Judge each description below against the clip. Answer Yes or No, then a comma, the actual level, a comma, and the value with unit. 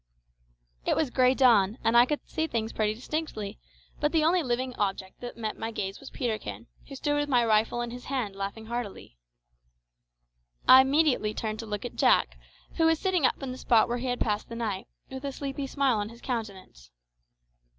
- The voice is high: Yes, high, 240 Hz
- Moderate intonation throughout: Yes, average, 4.1 semitones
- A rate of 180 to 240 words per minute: Yes, average, 200 wpm